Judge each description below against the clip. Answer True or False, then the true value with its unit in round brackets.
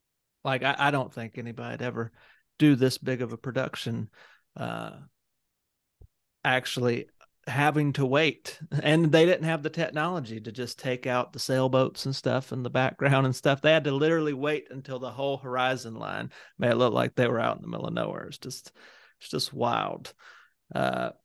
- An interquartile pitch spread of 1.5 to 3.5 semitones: True (3.0 semitones)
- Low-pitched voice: True (130 Hz)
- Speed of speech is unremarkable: True (185 wpm)